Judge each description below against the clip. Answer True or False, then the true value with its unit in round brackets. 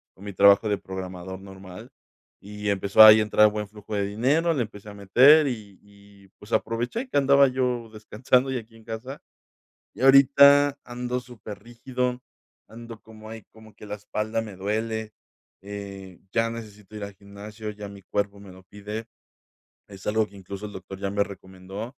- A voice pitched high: False (105 Hz)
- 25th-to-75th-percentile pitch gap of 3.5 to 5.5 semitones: False (2.7 semitones)